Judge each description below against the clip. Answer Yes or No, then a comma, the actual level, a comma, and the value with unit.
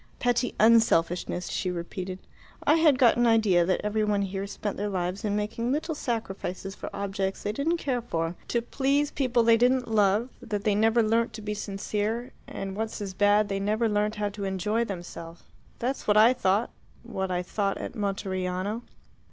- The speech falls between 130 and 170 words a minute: No, average, 180 wpm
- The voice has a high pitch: Yes, high, 210 Hz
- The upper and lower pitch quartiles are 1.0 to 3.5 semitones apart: Yes, average, 3.2 semitones